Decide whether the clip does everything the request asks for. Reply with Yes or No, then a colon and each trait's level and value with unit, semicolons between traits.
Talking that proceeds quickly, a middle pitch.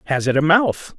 Yes: fast, 245 wpm; medium, 155 Hz